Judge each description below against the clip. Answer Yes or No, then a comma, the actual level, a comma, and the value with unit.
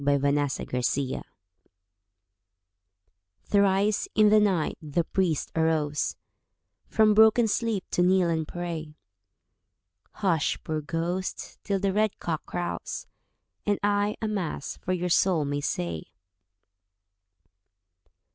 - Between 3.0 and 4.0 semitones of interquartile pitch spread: No, average, 4.9 semitones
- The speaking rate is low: Yes, slow, 110 wpm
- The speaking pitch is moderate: Yes, medium, 175 Hz